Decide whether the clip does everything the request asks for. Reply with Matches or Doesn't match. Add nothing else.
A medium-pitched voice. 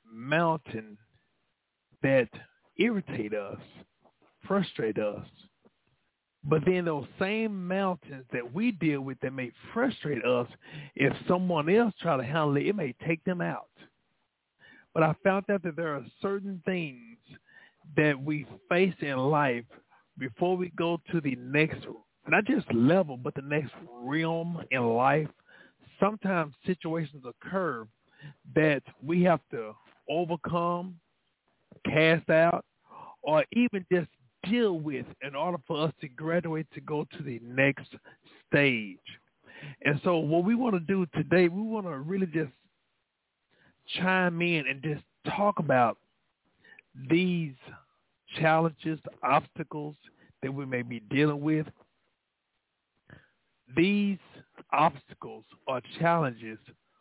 Matches